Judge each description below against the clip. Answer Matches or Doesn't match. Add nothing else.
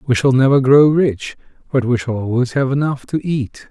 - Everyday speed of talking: Doesn't match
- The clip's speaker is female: Doesn't match